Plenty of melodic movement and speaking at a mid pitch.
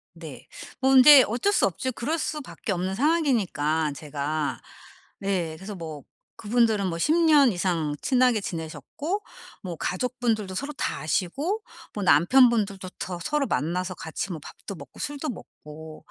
No: wide, 8.2 semitones; high, 200 Hz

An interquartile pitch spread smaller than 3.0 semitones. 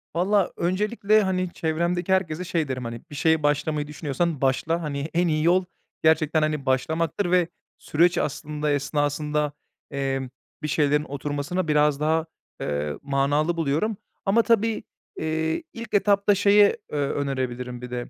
No: average, 3.7 semitones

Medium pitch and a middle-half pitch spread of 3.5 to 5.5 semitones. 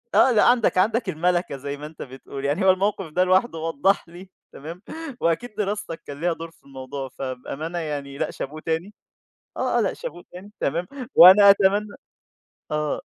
Yes: medium, 170 Hz; average, 5.1 semitones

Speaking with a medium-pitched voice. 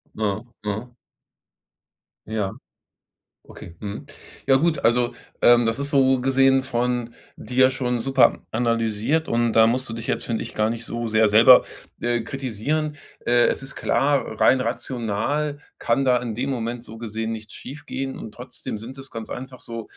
No: low, 120 Hz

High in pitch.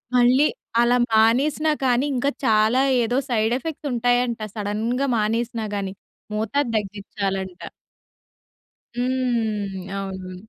Yes: high, 230 Hz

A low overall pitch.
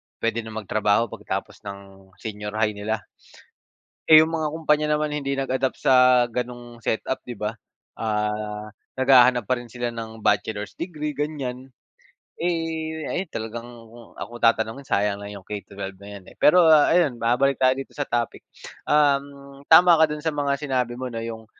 Yes: low, 125 Hz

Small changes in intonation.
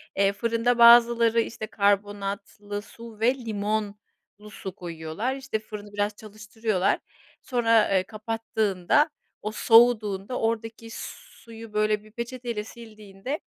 Yes: narrow, 2.2 semitones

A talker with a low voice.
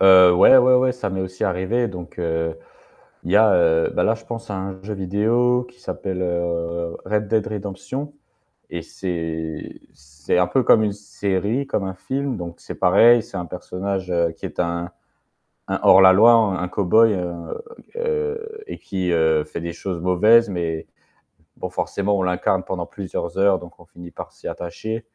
Yes: very low, 95 Hz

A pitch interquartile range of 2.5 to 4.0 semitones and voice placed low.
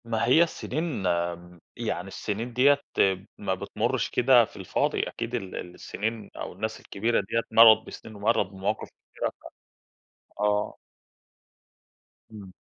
Yes: average, 3.4 semitones; low, 110 Hz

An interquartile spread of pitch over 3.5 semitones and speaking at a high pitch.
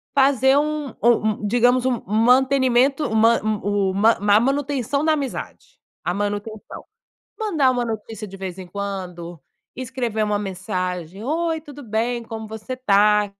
Yes: average, 4.5 semitones; high, 225 Hz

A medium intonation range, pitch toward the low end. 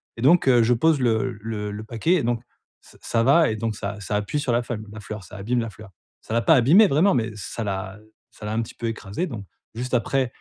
Yes: average, 3.3 semitones; low, 115 Hz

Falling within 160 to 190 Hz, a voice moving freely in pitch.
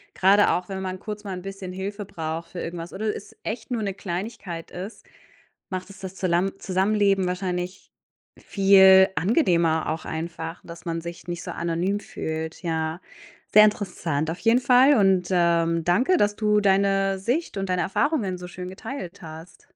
No: medium, 185 Hz; average, 2.9 semitones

